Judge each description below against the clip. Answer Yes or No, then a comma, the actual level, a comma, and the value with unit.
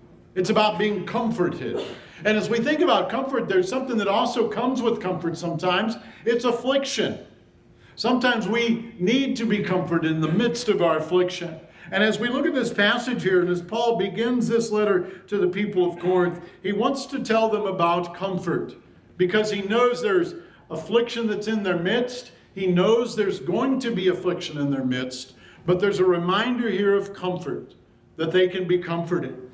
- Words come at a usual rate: Yes, average, 180 wpm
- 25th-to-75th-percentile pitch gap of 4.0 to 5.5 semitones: Yes, average, 4.4 semitones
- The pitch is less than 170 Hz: No, high, 200 Hz